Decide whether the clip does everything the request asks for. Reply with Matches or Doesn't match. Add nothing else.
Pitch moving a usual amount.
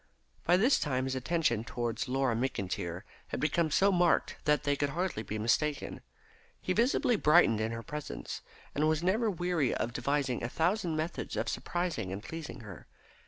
Doesn't match